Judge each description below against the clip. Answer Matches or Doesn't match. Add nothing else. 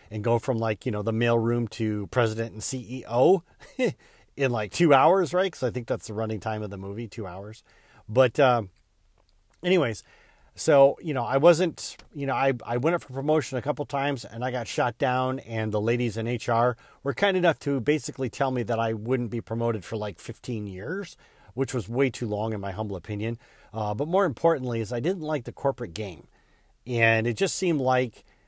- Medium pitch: Doesn't match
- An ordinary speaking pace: Doesn't match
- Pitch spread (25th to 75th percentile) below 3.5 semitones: Doesn't match